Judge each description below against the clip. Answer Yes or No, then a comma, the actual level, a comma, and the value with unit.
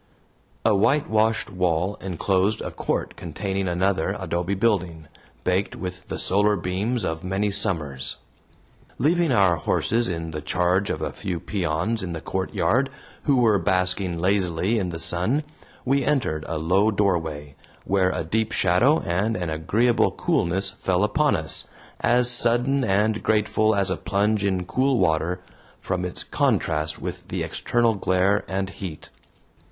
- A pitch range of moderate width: Yes, average, 3.8 semitones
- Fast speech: No, average, 145 wpm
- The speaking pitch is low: Yes, very low, 95 Hz